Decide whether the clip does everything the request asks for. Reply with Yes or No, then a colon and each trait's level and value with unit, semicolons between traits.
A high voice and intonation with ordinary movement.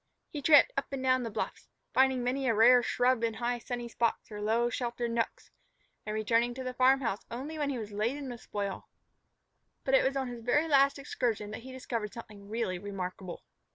Yes: high, 240 Hz; average, 3.0 semitones